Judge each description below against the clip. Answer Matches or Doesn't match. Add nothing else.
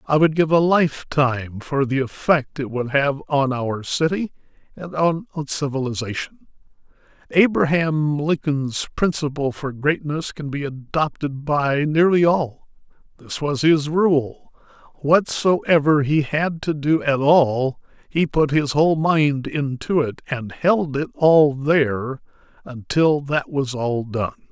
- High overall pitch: Doesn't match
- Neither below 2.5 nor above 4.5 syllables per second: Matches